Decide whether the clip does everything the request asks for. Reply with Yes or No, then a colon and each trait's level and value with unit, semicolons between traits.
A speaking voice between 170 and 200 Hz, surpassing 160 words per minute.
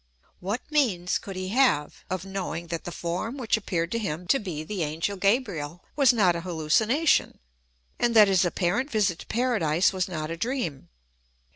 Yes: medium, 185 Hz; average, 175 wpm